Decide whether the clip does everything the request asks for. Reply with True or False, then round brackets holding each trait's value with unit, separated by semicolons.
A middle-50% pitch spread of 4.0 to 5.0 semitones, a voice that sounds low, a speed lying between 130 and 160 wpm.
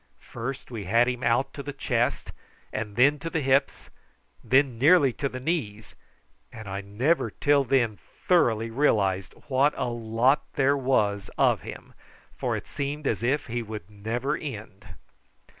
True (4.3 semitones; 125 Hz; 155 wpm)